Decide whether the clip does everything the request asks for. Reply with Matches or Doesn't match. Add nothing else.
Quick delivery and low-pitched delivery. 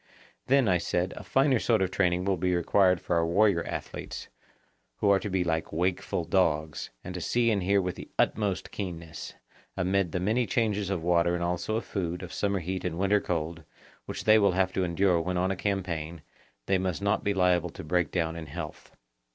Matches